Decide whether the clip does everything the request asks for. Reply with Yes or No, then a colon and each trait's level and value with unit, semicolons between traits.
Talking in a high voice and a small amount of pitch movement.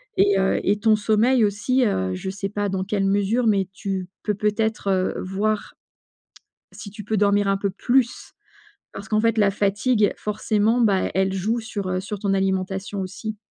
Yes: high, 205 Hz; narrow, 2.0 semitones